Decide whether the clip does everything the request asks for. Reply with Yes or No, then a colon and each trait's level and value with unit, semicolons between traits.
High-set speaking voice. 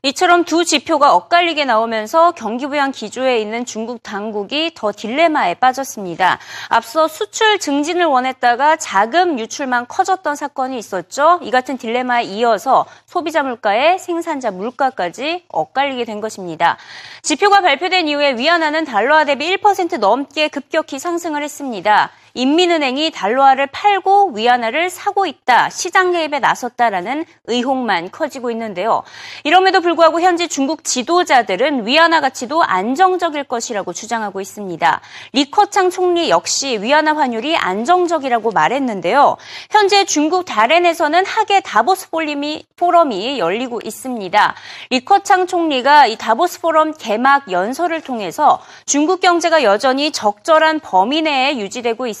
Yes: very high, 290 Hz